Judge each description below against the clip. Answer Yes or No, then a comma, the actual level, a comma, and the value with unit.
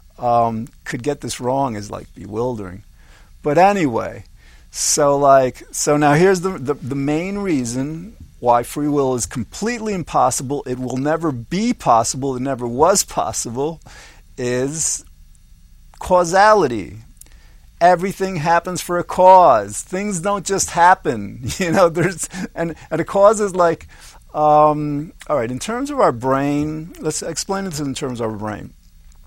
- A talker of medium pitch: Yes, medium, 145 Hz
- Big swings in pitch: Yes, wide, 6.6 semitones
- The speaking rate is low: No, average, 145 wpm